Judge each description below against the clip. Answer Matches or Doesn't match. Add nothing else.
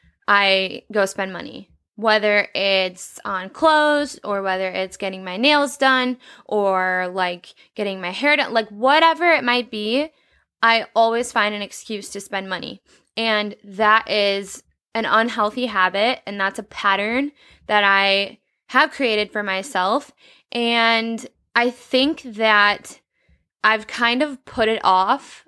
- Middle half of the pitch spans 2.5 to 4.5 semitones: Matches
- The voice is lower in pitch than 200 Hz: Doesn't match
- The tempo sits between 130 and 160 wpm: Matches